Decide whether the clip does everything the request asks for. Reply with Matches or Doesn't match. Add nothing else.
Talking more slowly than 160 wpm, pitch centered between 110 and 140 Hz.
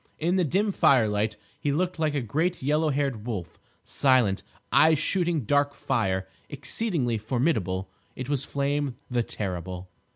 Matches